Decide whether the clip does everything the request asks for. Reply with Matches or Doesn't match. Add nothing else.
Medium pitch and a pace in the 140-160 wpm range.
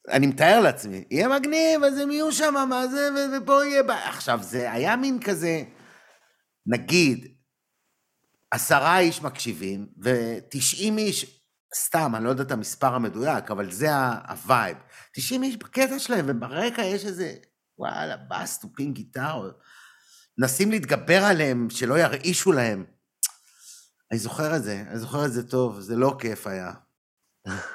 Matches